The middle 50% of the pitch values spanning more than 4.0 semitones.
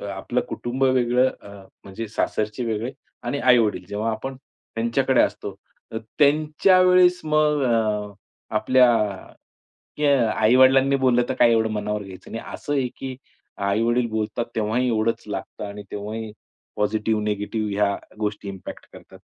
No: average, 3.7 semitones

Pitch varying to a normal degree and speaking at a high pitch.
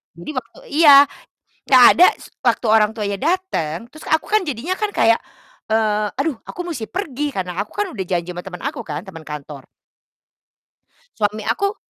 No: wide, 8.4 semitones; high, 225 Hz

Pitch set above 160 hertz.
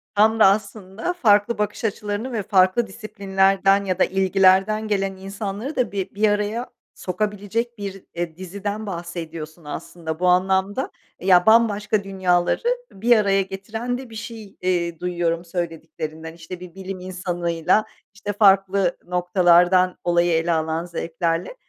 Yes: high, 190 Hz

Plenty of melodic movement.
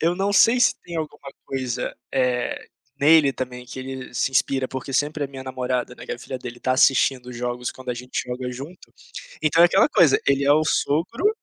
No: average, 3.6 semitones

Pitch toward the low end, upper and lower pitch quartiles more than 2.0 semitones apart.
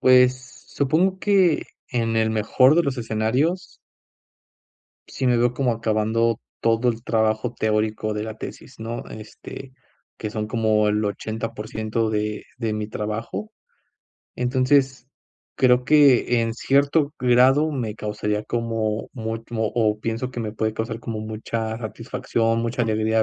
Yes: low, 115 Hz; narrow, 2.6 semitones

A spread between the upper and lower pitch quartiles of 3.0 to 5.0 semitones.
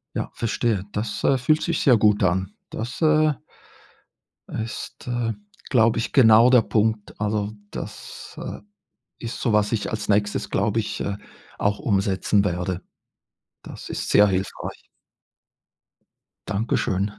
No: narrow, 2.5 semitones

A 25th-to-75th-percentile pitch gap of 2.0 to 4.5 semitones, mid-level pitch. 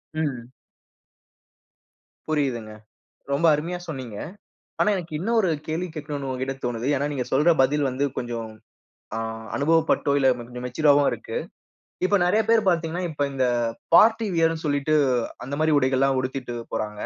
Yes: average, 4.0 semitones; medium, 145 Hz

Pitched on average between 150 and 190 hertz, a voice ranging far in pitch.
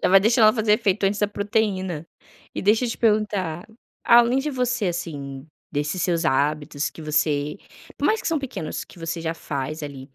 Yes: medium, 185 Hz; wide, 6.0 semitones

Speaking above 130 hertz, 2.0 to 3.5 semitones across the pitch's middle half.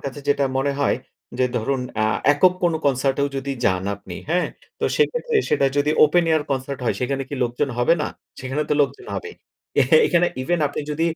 Yes: medium, 140 Hz; average, 3.1 semitones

